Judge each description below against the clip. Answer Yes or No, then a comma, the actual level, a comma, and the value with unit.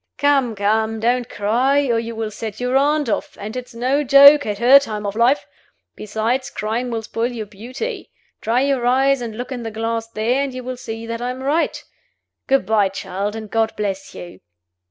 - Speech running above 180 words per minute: Yes, average, 200 wpm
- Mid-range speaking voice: No, high, 230 Hz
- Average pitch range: Yes, average, 3.0 semitones